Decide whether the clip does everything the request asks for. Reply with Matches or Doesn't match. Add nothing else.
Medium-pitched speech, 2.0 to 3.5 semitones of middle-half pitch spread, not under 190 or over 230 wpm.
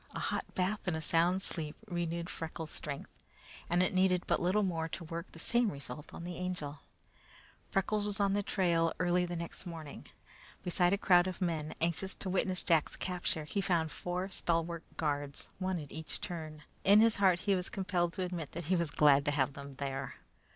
Matches